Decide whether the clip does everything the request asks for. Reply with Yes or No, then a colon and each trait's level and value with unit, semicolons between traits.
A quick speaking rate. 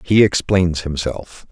No: slow, 120 wpm